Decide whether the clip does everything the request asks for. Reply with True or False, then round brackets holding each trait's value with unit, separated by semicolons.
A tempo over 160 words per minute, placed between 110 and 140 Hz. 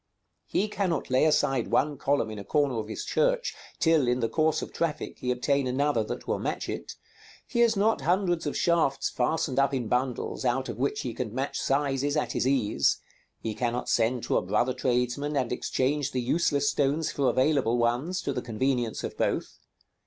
True (195 wpm; 135 Hz)